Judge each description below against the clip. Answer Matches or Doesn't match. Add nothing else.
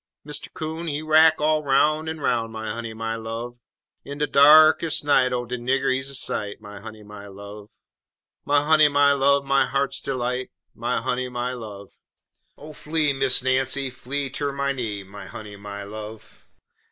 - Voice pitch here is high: Doesn't match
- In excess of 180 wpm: Doesn't match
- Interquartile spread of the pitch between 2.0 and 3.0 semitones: Doesn't match